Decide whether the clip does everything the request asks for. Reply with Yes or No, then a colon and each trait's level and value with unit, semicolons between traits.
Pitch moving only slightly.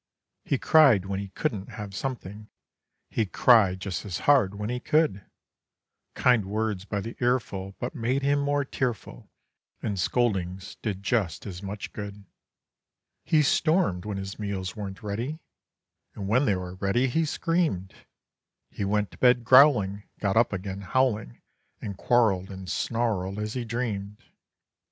No: average, 4.2 semitones